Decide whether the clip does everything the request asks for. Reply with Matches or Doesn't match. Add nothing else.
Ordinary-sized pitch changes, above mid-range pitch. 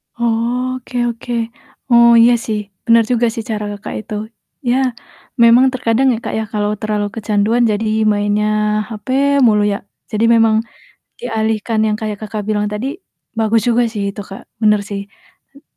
Doesn't match